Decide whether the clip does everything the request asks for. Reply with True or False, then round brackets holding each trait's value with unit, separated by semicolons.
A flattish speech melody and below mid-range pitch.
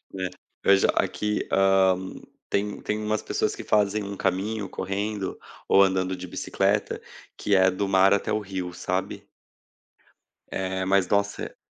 True (1.4 semitones; 95 Hz)